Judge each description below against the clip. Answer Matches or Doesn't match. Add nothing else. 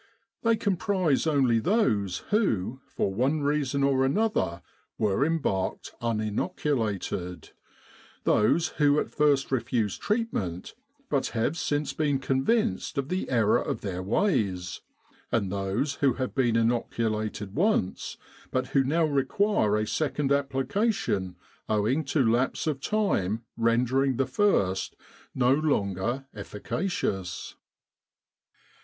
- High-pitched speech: Doesn't match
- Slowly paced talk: Matches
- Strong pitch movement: Matches